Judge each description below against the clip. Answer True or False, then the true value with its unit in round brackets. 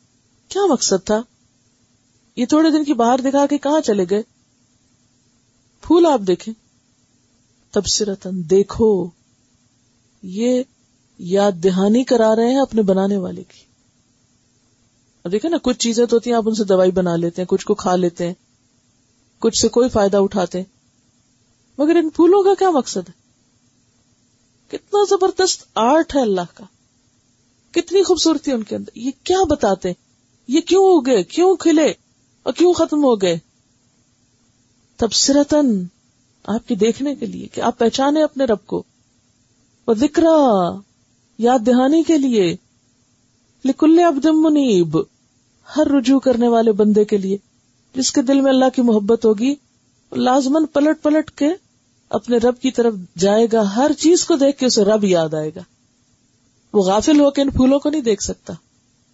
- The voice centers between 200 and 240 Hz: True (210 Hz)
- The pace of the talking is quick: False (150 wpm)